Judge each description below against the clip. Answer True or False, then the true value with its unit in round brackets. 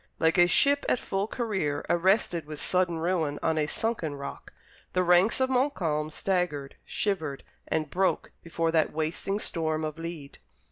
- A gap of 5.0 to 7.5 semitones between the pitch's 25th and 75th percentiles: False (3.8 semitones)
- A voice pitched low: False (170 Hz)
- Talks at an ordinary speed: True (155 wpm)